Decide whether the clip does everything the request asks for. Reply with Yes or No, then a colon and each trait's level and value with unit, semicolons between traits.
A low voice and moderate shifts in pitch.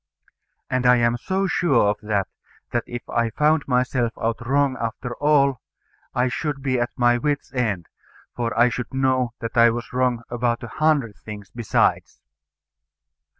No: low, 120 Hz; narrow, 2.3 semitones